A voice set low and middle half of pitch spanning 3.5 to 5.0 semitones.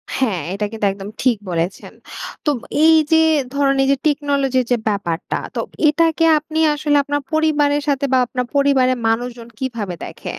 No: very high, 270 Hz; average, 4.2 semitones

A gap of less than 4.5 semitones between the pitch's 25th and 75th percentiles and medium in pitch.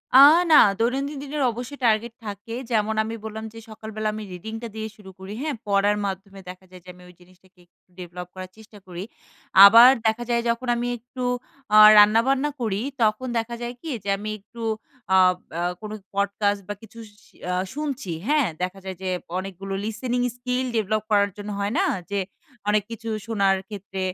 No: average, 3.1 semitones; high, 215 Hz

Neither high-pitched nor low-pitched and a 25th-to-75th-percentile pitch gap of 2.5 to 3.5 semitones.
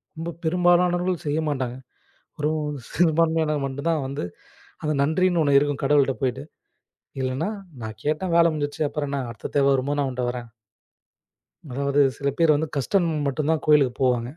Yes: medium, 145 Hz; average, 3.0 semitones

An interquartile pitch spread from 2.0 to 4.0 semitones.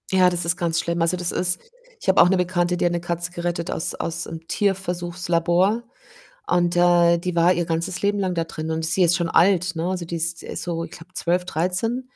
No: narrow, 1.3 semitones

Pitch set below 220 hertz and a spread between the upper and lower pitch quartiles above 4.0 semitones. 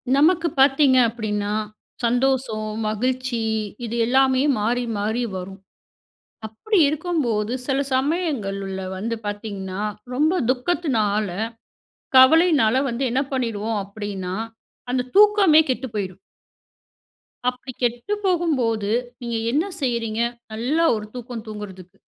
No: high, 240 Hz; average, 4.4 semitones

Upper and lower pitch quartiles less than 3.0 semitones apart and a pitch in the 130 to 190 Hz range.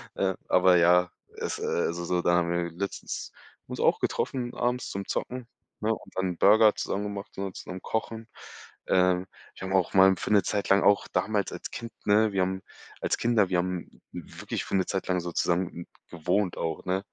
No: narrow, 2.5 semitones; very low, 95 Hz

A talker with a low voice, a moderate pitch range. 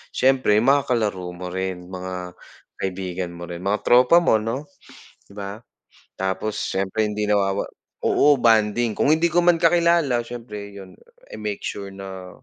Yes: low, 105 Hz; average, 4.7 semitones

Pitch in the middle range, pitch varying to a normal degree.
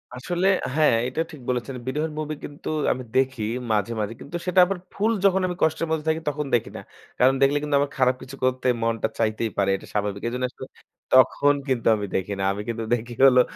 No: low, 130 Hz; average, 4.7 semitones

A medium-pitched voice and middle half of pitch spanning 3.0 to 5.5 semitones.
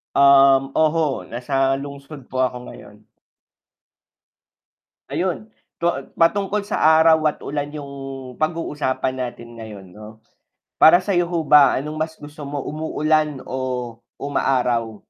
Yes: medium, 145 Hz; average, 3.4 semitones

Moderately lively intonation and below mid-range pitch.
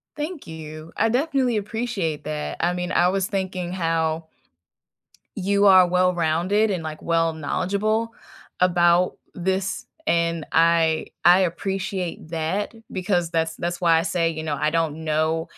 No: average, 3.0 semitones; medium, 175 Hz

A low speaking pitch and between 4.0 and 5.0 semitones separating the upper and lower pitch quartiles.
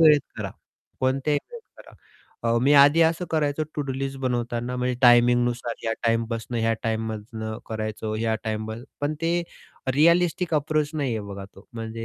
Yes: low, 125 Hz; average, 4.5 semitones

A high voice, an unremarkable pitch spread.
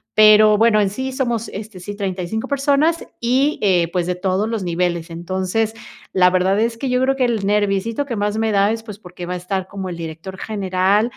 Yes: high, 205 Hz; average, 3.6 semitones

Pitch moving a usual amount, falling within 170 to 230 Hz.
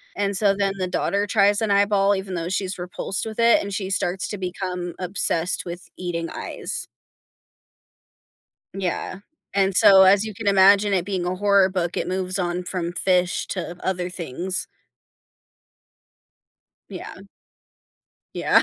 No: narrow, 1.8 semitones; high, 190 Hz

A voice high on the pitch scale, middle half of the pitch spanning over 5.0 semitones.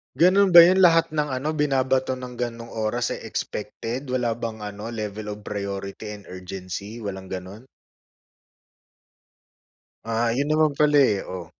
No: low, 115 Hz; wide, 5.6 semitones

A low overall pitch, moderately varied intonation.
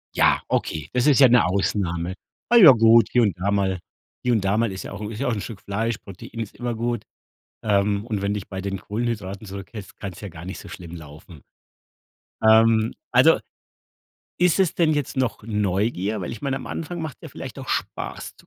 Yes: low, 105 Hz; average, 3.5 semitones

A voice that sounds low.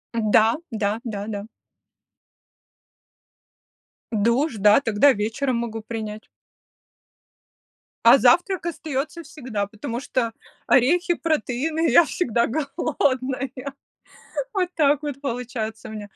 No: high, 245 Hz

